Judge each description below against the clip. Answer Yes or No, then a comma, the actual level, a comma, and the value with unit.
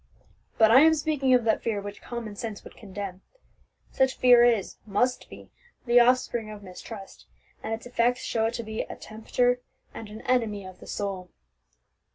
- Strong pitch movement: No, average, 3.2 semitones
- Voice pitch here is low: No, high, 225 Hz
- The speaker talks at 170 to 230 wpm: Yes, average, 180 wpm